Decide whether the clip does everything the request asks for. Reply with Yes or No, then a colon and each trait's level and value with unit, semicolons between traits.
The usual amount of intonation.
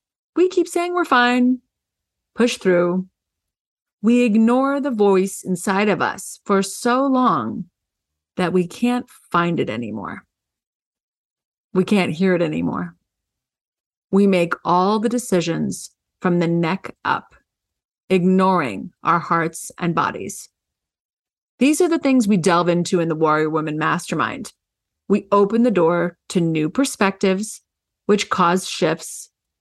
No: wide, 5.7 semitones